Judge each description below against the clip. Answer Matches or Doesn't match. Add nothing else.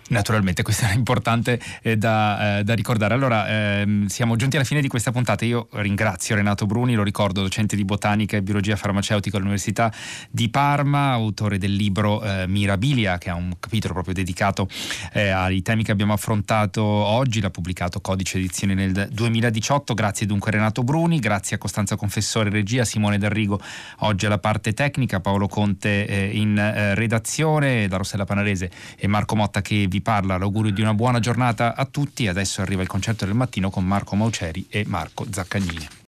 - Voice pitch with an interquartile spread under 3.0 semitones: Matches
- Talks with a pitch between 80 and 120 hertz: Matches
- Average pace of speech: Doesn't match